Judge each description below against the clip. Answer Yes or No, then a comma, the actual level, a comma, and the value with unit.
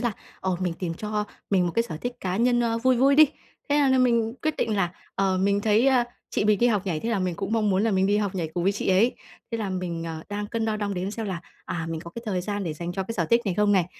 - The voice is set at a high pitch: Yes, high, 205 Hz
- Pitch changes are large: No, average, 3.9 semitones